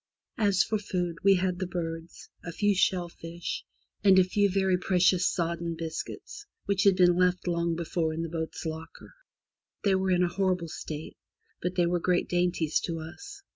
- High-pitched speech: No, medium, 180 Hz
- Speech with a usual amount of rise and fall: No, narrow, 2.1 semitones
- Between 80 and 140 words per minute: No, average, 175 wpm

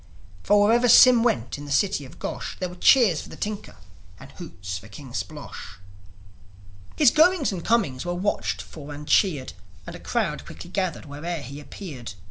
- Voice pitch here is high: No, medium, 165 Hz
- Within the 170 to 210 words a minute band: Yes, average, 180 wpm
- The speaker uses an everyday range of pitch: No, wide, 7.2 semitones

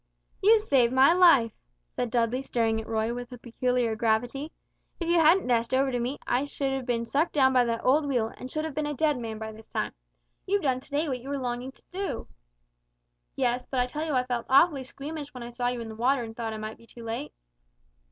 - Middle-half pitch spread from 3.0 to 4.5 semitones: Yes, average, 3.4 semitones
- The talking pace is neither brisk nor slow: No, fast, 240 wpm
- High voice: Yes, very high, 250 Hz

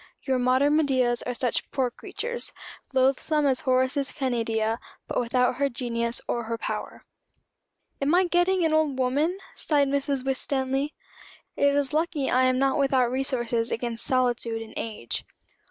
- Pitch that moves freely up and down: No, average, 2.8 semitones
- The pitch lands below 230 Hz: No, very high, 260 Hz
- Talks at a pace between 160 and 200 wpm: No, average, 150 wpm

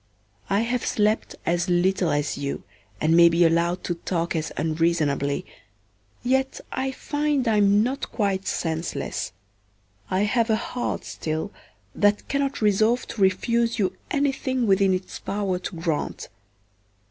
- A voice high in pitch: Yes, high, 195 Hz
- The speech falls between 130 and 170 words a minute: Yes, average, 140 wpm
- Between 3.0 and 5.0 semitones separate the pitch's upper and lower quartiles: No, wide, 5.5 semitones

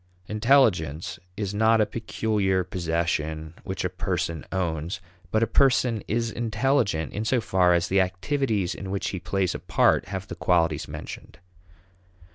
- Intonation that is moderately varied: Yes, average, 4.4 semitones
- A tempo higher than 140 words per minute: Yes, average, 150 wpm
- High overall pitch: No, very low, 95 Hz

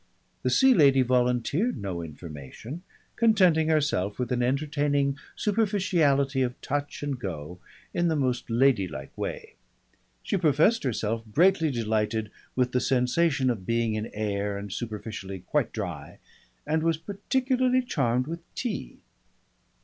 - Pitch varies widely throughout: Yes, wide, 6.6 semitones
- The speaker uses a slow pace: Yes, slow, 130 wpm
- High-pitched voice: No, low, 130 Hz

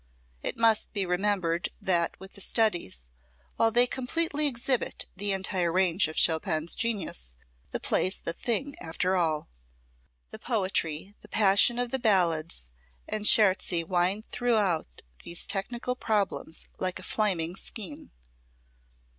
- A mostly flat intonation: No, average, 4.9 semitones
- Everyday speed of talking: No, slow, 130 wpm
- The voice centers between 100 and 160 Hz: No, high, 190 Hz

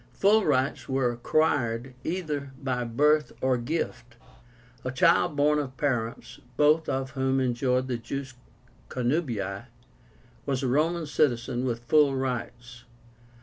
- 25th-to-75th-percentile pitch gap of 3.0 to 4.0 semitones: Yes, average, 3.4 semitones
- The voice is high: No, low, 130 Hz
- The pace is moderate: No, slow, 125 wpm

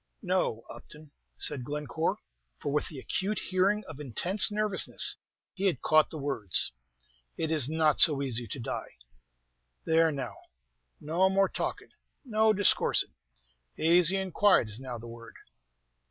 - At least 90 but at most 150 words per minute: Yes, average, 140 wpm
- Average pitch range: No, wide, 6.1 semitones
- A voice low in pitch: No, medium, 155 Hz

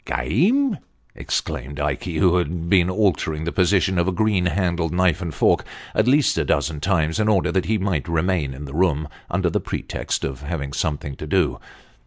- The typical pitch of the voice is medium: No, very low, 85 Hz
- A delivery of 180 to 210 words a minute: Yes, average, 200 wpm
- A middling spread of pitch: Yes, average, 4.0 semitones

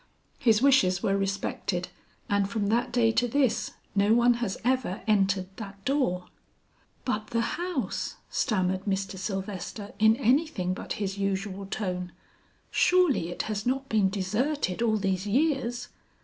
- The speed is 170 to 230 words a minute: No, average, 140 wpm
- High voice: Yes, high, 210 Hz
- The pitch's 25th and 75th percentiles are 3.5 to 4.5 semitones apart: Yes, average, 4.0 semitones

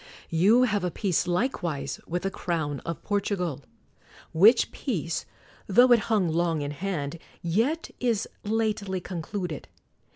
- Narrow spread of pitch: No, average, 4.3 semitones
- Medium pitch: Yes, medium, 180 Hz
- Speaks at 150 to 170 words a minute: No, average, 140 wpm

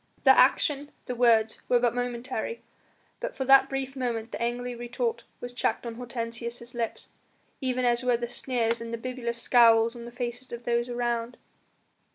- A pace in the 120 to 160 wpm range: No, average, 175 wpm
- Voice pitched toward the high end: Yes, high, 240 Hz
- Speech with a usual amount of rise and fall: No, narrow, 1.2 semitones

